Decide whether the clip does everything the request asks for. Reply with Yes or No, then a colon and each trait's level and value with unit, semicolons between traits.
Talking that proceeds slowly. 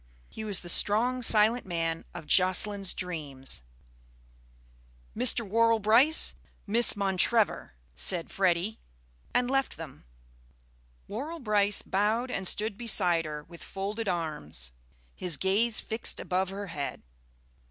Yes: slow, 120 wpm